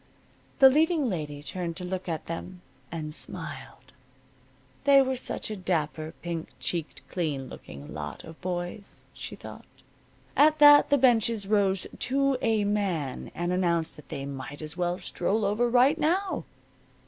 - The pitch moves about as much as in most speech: No, wide, 7.2 semitones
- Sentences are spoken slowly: No, average, 150 wpm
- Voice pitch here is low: No, medium, 185 Hz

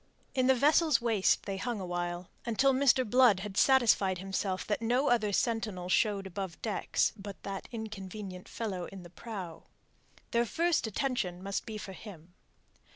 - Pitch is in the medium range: No, high, 210 Hz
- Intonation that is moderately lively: Yes, average, 4.1 semitones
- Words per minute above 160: No, average, 155 wpm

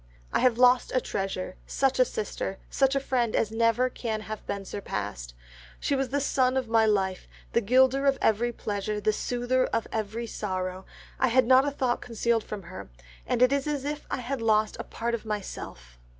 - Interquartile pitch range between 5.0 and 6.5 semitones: No, average, 3.7 semitones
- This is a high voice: Yes, high, 230 Hz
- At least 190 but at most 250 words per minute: Yes, average, 200 wpm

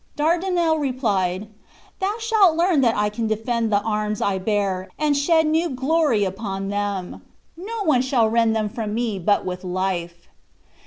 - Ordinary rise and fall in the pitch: No, wide, 7.3 semitones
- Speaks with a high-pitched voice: Yes, high, 225 Hz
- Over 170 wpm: No, average, 160 wpm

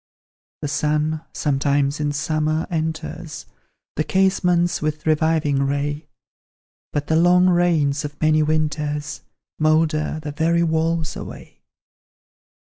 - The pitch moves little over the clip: Yes, narrow, 1.6 semitones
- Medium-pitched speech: Yes, medium, 155 Hz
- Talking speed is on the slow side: Yes, slow, 110 wpm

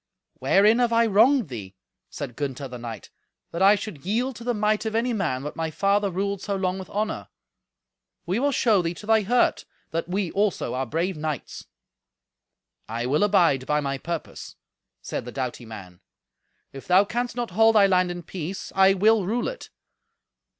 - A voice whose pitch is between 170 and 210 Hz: Yes, high, 190 Hz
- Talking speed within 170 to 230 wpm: Yes, average, 185 wpm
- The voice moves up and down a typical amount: No, wide, 6.3 semitones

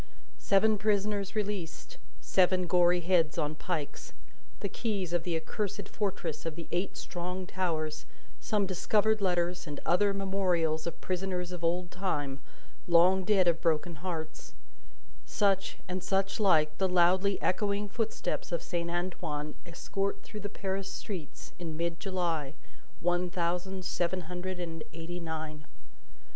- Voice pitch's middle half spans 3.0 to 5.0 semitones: No, narrow, 2.5 semitones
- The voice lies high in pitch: No, medium, 180 Hz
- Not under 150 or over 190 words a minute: No, average, 140 wpm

